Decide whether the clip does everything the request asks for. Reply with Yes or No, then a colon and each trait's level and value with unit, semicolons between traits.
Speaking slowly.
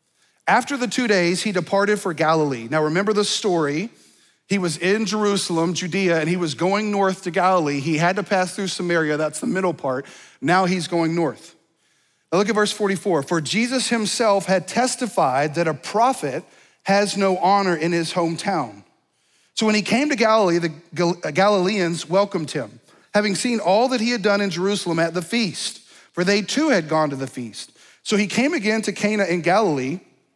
No: average, 190 wpm